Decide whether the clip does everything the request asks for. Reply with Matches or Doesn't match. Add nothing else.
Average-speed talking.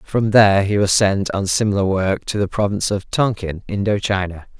Matches